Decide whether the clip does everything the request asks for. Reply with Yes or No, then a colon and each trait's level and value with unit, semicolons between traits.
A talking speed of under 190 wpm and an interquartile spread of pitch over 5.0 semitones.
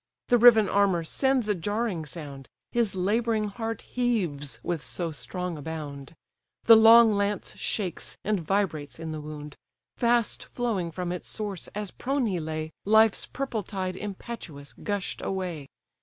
Yes: average, 150 wpm; wide, 5.5 semitones